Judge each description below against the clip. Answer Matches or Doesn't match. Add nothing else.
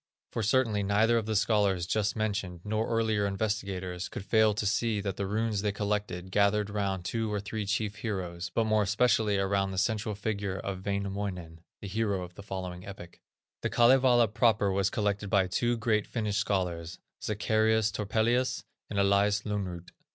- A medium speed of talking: Matches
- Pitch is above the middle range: Doesn't match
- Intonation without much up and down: Matches